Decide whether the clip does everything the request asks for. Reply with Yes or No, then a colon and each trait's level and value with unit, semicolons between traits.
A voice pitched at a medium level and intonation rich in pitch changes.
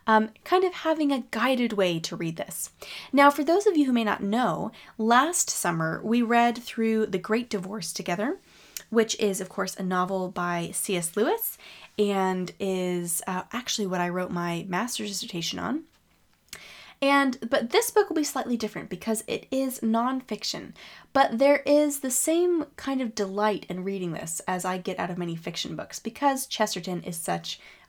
No: high, 220 Hz; wide, 6.2 semitones